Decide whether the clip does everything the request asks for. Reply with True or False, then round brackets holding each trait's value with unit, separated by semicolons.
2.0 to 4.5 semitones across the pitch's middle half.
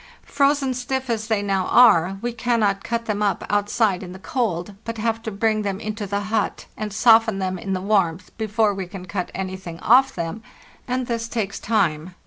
True (3.2 semitones)